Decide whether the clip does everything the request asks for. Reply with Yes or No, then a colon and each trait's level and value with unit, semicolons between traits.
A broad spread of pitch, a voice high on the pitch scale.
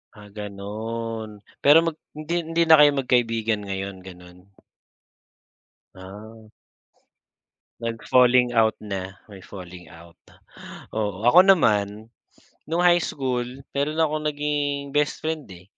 No: wide, 6.3 semitones; low, 115 Hz